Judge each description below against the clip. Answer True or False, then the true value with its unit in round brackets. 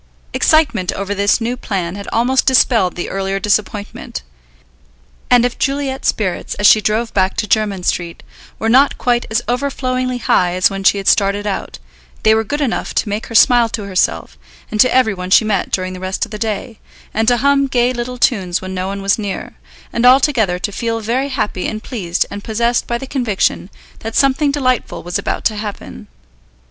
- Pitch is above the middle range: True (220 Hz)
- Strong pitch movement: False (4.0 semitones)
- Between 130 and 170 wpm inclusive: False (195 wpm)